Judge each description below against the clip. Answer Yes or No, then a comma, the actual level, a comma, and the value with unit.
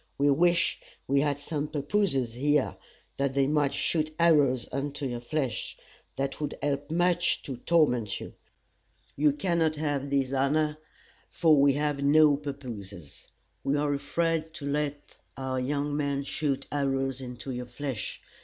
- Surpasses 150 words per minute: No, average, 145 wpm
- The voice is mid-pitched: Yes, medium, 145 Hz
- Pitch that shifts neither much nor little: No, narrow, 2.0 semitones